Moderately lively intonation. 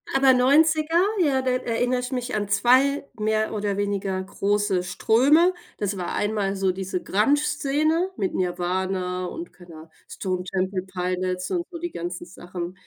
No: wide, 6.3 semitones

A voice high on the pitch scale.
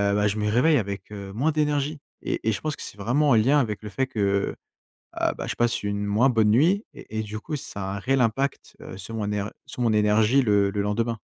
No: low, 110 Hz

